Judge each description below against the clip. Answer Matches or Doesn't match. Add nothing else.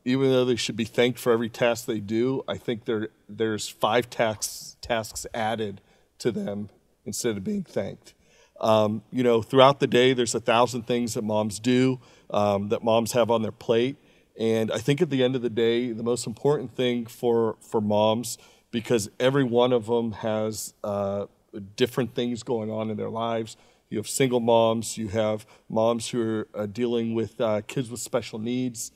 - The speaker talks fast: Doesn't match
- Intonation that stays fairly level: Matches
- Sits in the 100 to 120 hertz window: Matches